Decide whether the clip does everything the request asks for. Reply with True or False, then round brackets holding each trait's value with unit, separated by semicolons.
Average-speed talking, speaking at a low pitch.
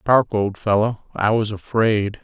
True (160 wpm; 110 Hz)